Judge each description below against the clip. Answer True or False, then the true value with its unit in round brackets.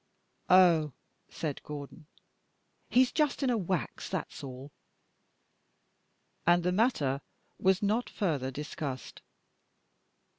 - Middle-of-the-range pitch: True (170 Hz)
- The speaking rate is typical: False (100 wpm)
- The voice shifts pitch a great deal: True (5.8 semitones)